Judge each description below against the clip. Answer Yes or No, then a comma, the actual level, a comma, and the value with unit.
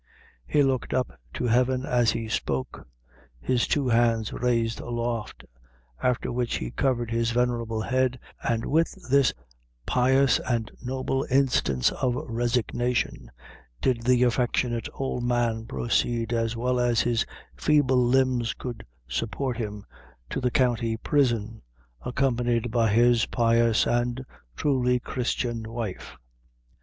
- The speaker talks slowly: Yes, slow, 125 wpm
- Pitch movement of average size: No, narrow, 1.7 semitones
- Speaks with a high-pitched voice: No, low, 120 Hz